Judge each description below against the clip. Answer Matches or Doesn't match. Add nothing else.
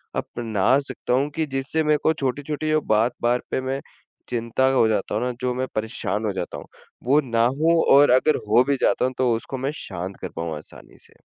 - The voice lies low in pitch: Matches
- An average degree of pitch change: Matches